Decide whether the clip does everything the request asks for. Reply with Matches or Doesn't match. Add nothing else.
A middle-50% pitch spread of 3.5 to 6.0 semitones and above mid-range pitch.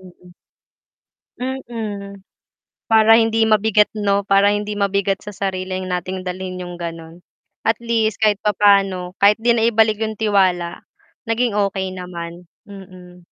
Doesn't match